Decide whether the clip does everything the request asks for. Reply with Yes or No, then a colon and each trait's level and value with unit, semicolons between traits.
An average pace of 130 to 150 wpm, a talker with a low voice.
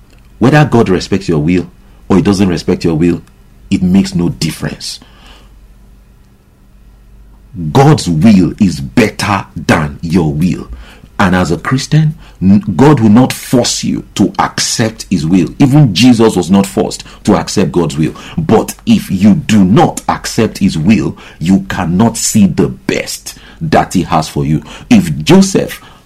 Yes: average, 145 wpm; low, 100 Hz